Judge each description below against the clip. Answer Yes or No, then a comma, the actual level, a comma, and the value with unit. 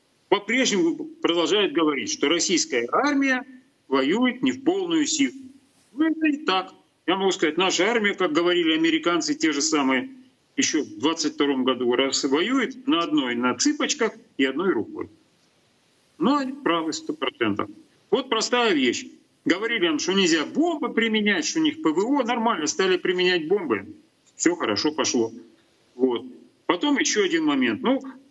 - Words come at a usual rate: Yes, average, 145 wpm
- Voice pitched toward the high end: Yes, very high, 260 Hz